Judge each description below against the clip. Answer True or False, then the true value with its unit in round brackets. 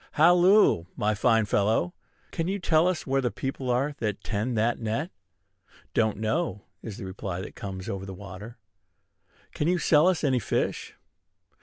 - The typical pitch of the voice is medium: False (115 Hz)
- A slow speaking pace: False (165 wpm)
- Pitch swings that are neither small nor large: False (7.4 semitones)